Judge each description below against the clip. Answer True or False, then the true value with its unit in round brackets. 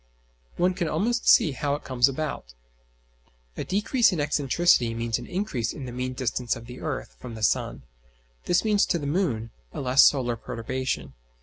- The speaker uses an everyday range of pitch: False (6.5 semitones)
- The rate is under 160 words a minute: False (175 wpm)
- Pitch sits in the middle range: False (130 Hz)